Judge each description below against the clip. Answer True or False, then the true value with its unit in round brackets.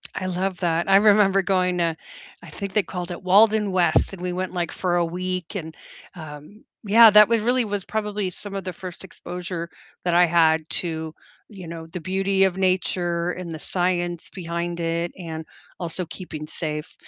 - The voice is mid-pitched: True (180 Hz)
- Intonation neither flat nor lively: False (2.3 semitones)